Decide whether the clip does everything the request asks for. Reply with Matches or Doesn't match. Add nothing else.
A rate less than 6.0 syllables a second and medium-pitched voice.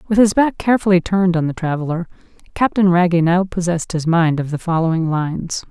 Doesn't match